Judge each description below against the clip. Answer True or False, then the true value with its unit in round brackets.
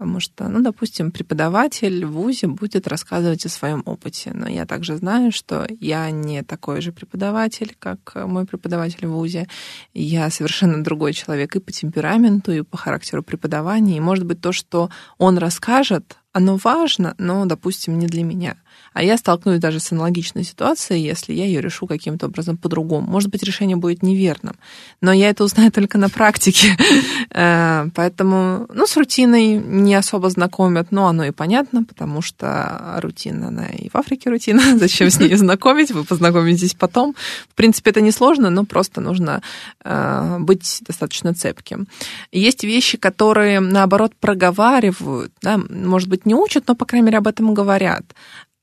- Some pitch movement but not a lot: True (4.1 semitones)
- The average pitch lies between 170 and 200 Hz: True (190 Hz)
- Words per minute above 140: True (160 wpm)